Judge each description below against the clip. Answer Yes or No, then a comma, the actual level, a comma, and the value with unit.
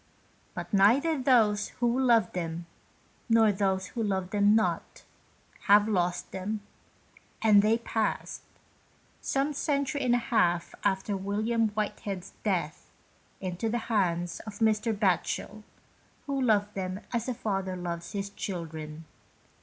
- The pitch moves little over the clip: No, average, 3.3 semitones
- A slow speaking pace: Yes, slow, 130 wpm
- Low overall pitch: No, high, 205 Hz